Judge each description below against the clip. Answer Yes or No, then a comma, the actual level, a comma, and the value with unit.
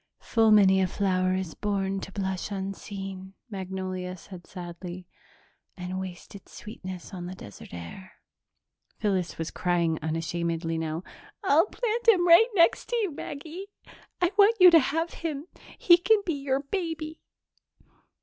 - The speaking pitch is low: No, high, 195 Hz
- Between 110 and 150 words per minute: Yes, average, 145 wpm